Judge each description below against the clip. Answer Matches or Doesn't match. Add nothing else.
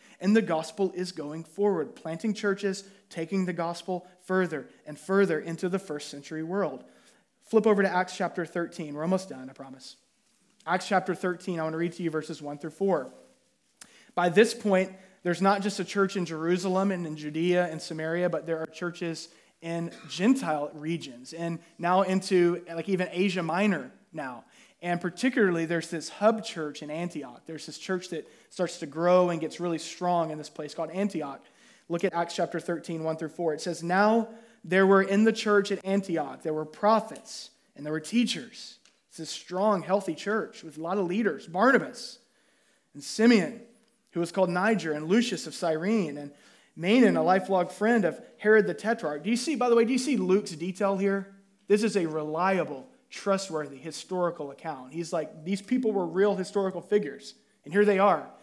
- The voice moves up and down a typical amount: Matches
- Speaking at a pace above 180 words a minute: Matches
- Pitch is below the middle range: Doesn't match